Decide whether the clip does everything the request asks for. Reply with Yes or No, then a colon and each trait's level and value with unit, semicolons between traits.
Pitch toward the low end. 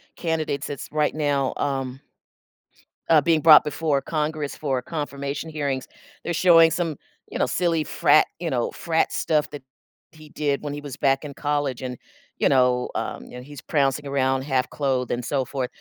No: medium, 145 Hz